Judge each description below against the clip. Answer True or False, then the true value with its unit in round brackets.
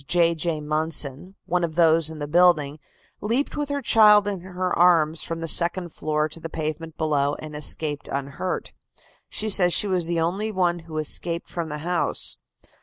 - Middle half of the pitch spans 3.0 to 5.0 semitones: False (2.6 semitones)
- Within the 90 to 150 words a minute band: False (180 wpm)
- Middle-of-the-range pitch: True (165 Hz)